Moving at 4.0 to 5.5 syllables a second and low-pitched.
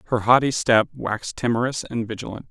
No: 6.1 syllables/s; low, 120 Hz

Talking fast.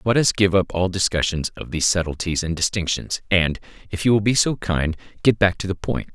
Yes: fast, 235 wpm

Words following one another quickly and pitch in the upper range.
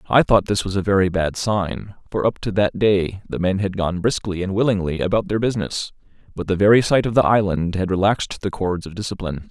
No: fast, 225 wpm; low, 100 Hz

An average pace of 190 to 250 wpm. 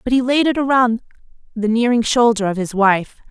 Yes: average, 200 wpm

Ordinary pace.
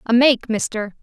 Yes: average, 175 wpm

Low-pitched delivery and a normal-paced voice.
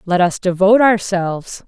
No: high, 190 Hz; average, 145 wpm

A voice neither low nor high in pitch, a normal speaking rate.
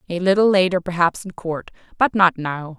Yes: medium, 180 Hz; average, 170 wpm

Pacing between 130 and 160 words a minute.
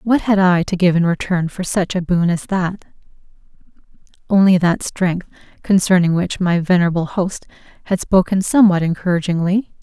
Yes: average, 155 wpm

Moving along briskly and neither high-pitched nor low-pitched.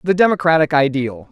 No: slow, 135 wpm; medium, 155 Hz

